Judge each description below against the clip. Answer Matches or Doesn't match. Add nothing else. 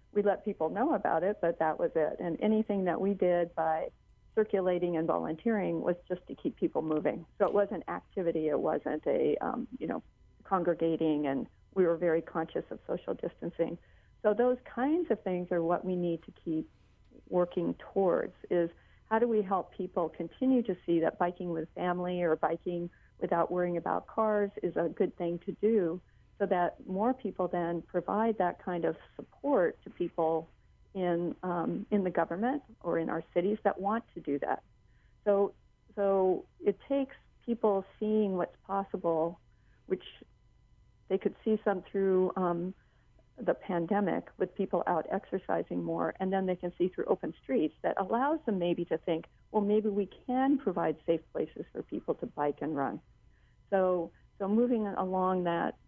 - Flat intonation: Doesn't match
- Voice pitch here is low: Doesn't match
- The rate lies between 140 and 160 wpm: Doesn't match